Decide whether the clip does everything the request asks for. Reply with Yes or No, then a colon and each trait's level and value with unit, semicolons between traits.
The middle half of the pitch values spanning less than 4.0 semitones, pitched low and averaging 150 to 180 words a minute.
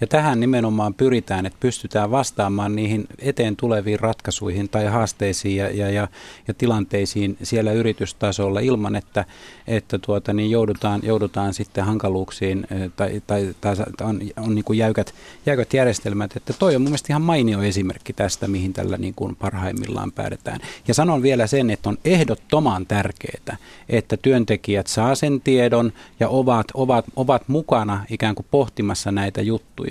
Yes: average, 3.6 semitones; low, 110 Hz; fast, 155 wpm